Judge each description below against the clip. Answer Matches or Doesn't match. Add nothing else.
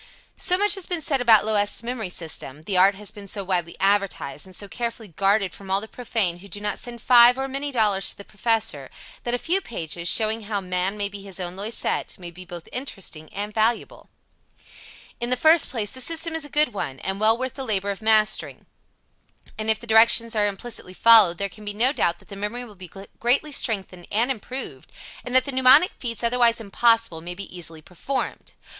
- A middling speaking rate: Doesn't match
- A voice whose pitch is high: Matches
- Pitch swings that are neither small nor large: Matches